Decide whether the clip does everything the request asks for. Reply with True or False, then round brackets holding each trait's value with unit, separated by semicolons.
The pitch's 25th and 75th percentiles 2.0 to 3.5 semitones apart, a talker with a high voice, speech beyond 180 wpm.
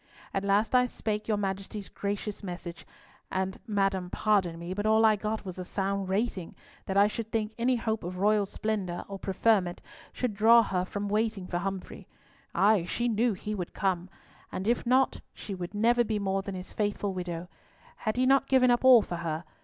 True (2.7 semitones; 205 Hz; 195 wpm)